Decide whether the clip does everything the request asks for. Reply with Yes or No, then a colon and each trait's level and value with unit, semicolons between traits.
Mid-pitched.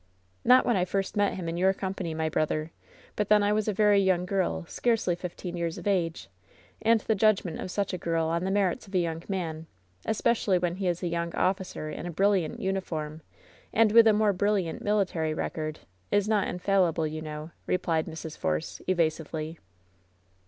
Yes: medium, 180 Hz